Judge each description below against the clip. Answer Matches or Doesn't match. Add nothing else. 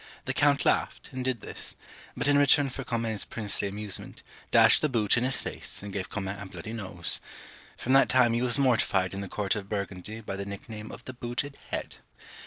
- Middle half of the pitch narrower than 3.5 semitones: Doesn't match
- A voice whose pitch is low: Matches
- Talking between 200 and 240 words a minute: Matches